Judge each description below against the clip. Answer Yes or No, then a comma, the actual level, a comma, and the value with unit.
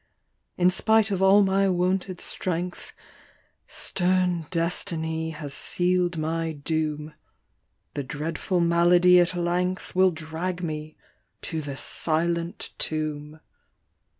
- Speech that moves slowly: Yes, slow, 110 wpm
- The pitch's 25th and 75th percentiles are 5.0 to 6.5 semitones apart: No, narrow, 2.4 semitones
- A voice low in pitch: No, medium, 170 Hz